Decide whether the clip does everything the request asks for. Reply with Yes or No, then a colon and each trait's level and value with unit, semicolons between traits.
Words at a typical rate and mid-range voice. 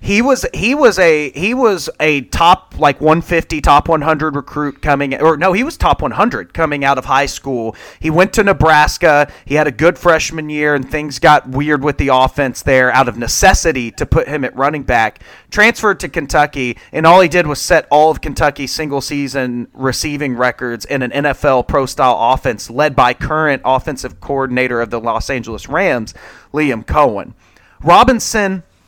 Yes: average, 180 wpm; medium, 145 Hz